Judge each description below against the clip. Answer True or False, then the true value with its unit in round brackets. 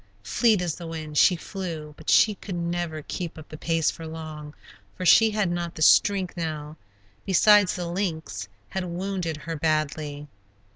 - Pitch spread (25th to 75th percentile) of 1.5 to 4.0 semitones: True (2.8 semitones)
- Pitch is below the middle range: False (165 Hz)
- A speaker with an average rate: True (165 wpm)